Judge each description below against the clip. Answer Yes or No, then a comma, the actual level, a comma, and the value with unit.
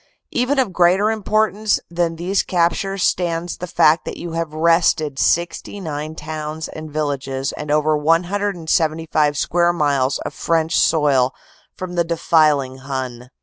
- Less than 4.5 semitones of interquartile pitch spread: Yes, average, 2.8 semitones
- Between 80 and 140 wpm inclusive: Yes, slow, 135 wpm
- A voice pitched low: No, medium, 165 Hz